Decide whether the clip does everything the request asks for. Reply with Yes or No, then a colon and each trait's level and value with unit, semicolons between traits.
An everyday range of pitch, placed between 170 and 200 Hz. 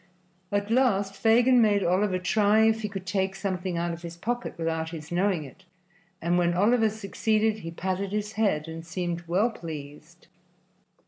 Yes: average, 3.9 semitones; high, 190 Hz